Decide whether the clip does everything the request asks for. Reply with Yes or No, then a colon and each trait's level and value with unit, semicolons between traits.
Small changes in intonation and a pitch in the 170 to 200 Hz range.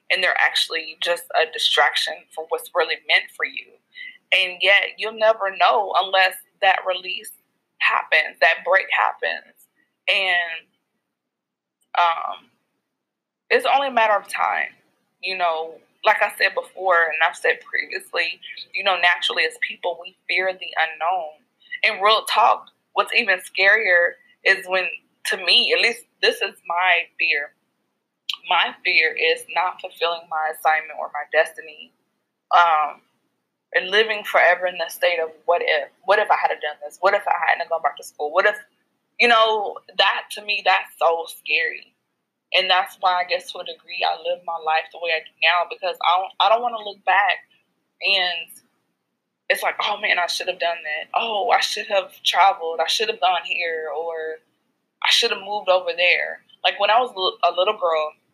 No: average, 4.6 semitones; medium, 185 Hz